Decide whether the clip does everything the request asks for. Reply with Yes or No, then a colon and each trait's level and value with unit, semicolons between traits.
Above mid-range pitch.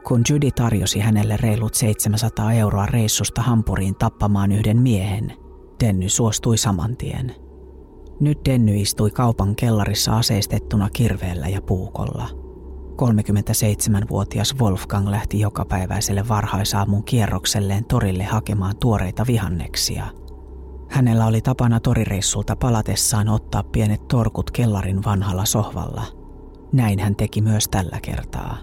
No: low, 105 Hz